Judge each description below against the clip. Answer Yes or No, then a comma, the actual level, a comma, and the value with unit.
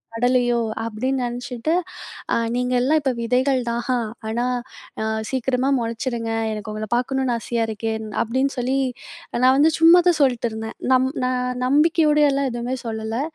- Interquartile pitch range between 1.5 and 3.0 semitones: Yes, narrow, 2.4 semitones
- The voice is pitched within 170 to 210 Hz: No, very high, 250 Hz